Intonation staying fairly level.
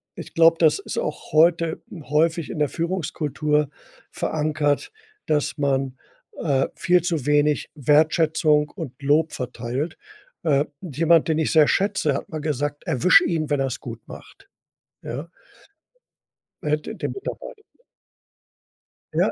Yes: narrow, 2.2 semitones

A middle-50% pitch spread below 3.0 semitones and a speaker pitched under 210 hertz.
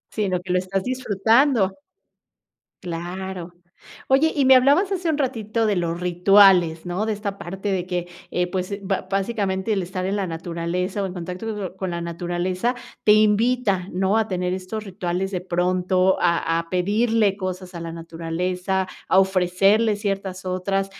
Yes: narrow, 2.6 semitones; high, 190 Hz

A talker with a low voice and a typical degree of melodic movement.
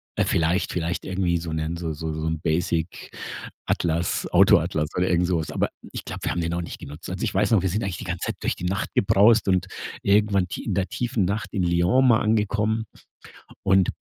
Yes: very low, 90 Hz; average, 3.1 semitones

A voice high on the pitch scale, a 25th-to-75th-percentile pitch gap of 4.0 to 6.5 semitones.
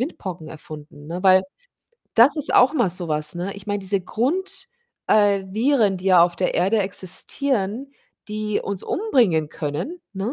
Yes: high, 195 Hz; average, 4.8 semitones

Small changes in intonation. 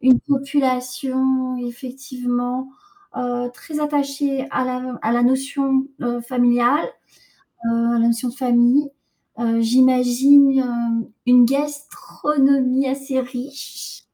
Yes: narrow, 1.9 semitones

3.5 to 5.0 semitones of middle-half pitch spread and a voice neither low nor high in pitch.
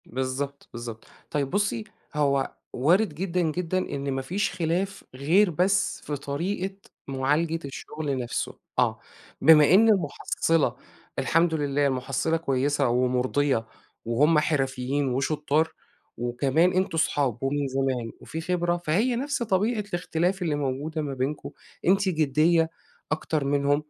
Yes: average, 4.3 semitones; medium, 150 Hz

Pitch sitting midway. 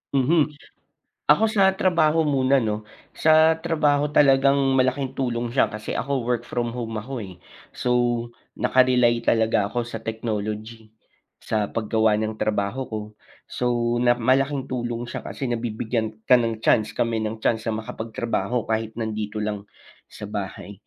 No: low, 120 Hz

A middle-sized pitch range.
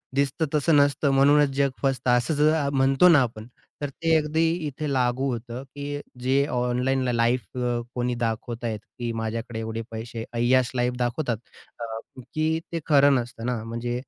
Yes: average, 3.1 semitones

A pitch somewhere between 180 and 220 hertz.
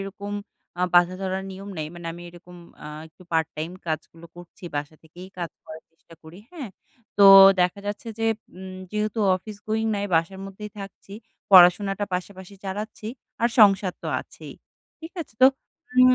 Yes: high, 190 Hz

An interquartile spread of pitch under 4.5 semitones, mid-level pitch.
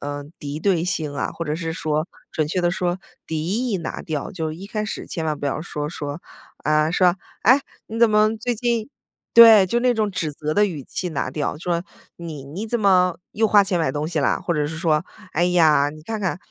No: average, 4.8 semitones; medium, 170 Hz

